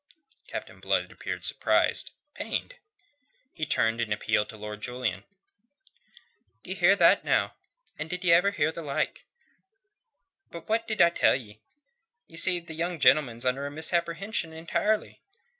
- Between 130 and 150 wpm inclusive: Yes, average, 145 wpm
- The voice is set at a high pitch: No, medium, 160 Hz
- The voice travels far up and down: Yes, wide, 6.3 semitones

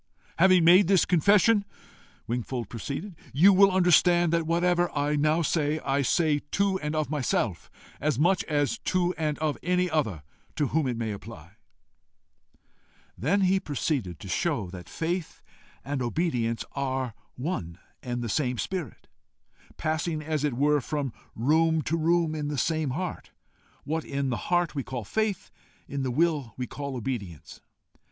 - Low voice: No, medium, 150 Hz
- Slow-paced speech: No, average, 155 wpm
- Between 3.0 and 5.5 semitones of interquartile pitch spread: Yes, average, 5.1 semitones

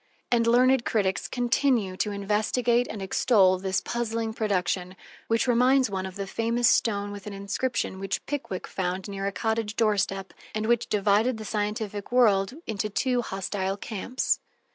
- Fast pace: No, average, 155 wpm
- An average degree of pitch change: Yes, average, 3.3 semitones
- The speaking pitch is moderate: No, high, 210 Hz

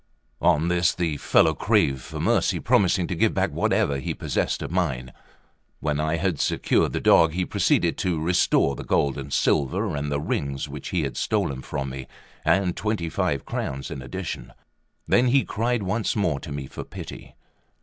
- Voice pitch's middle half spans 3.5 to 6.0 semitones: Yes, average, 4.7 semitones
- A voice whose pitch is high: No, very low, 80 Hz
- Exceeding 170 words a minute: Yes, average, 180 wpm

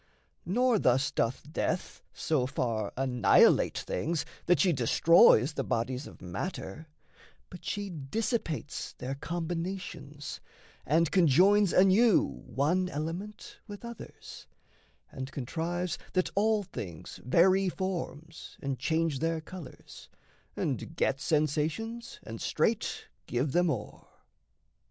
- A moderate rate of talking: No, slow, 110 wpm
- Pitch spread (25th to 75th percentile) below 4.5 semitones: No, wide, 5.6 semitones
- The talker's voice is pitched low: No, medium, 165 Hz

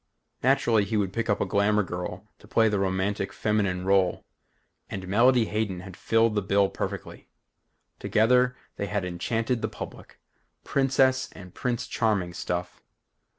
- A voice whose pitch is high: No, low, 105 Hz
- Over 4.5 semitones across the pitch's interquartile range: No, average, 3.2 semitones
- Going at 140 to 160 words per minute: Yes, average, 145 wpm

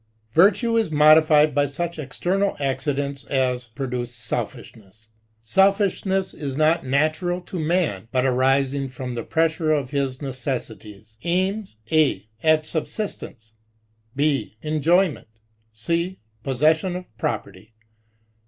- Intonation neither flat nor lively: Yes, average, 4.9 semitones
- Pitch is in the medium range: Yes, medium, 145 Hz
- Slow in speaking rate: Yes, slow, 110 wpm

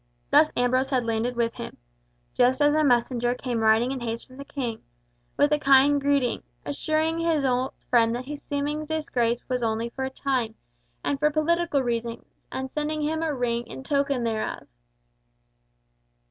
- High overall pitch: Yes, very high, 265 Hz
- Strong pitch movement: No, average, 3.5 semitones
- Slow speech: No, average, 170 wpm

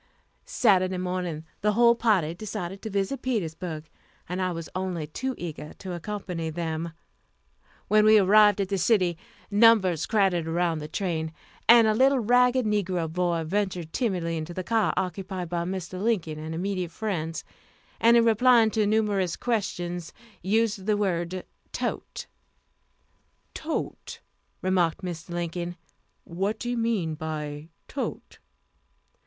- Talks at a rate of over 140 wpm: No, slow, 135 wpm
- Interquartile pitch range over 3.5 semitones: Yes, average, 4.0 semitones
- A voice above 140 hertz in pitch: Yes, medium, 185 Hz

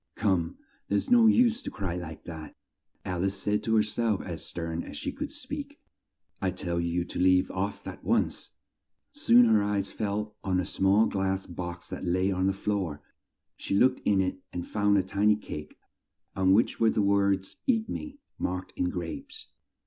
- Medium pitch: No, very low, 95 Hz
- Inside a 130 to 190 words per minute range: Yes, average, 185 wpm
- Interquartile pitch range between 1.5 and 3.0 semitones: Yes, average, 2.7 semitones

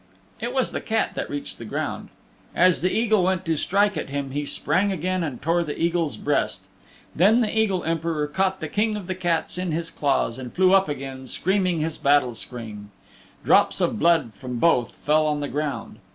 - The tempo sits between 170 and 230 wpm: Yes, average, 200 wpm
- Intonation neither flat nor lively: Yes, average, 4.7 semitones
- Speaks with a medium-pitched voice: Yes, medium, 165 Hz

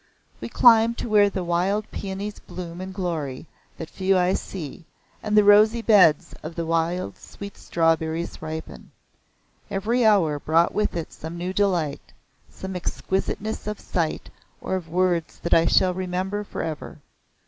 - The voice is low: No, medium, 185 Hz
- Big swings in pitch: No, average, 3.6 semitones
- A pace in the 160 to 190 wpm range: No, average, 150 wpm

